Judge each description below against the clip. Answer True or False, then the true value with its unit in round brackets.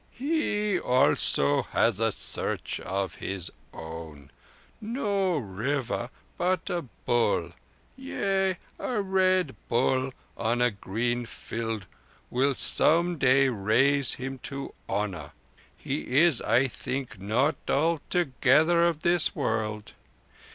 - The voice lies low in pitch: True (130 Hz)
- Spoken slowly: True (110 wpm)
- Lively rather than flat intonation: True (7.6 semitones)